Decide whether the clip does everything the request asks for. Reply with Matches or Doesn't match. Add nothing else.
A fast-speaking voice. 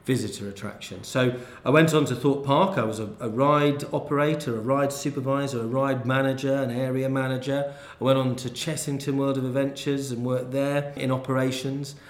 Doesn't match